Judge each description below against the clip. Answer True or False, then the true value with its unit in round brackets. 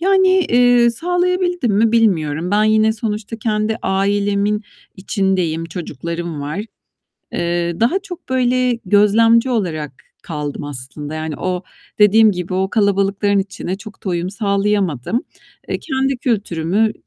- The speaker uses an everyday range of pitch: True (4.8 semitones)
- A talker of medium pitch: False (205 Hz)